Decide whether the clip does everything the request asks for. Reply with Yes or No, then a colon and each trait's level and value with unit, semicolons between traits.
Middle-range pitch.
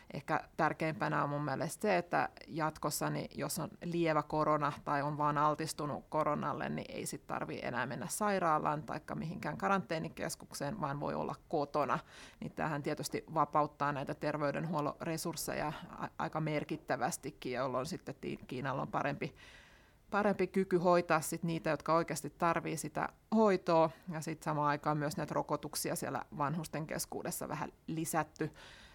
Yes: medium, 155 Hz